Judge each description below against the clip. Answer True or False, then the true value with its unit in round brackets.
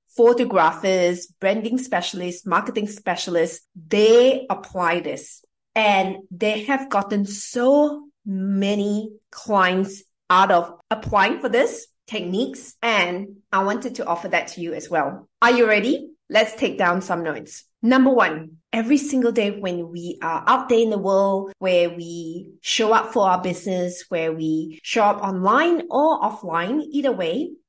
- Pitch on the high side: True (200 Hz)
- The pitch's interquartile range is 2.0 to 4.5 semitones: False (5.1 semitones)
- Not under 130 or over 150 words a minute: True (145 wpm)